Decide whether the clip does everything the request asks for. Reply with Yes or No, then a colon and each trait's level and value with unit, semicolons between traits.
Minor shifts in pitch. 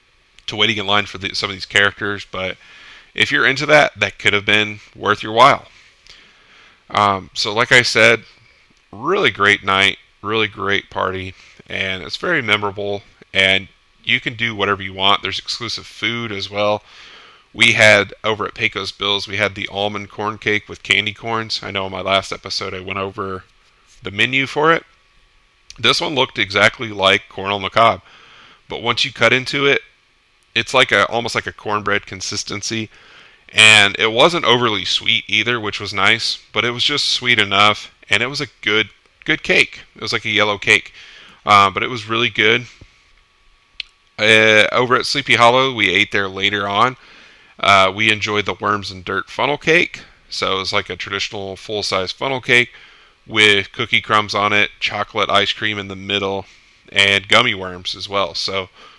Yes: narrow, 2.2 semitones